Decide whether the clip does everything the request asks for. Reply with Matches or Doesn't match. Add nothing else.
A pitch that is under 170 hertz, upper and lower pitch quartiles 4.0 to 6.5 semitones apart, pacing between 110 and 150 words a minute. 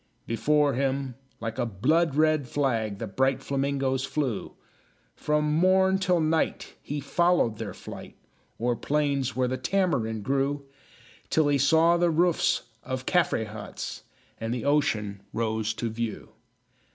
Matches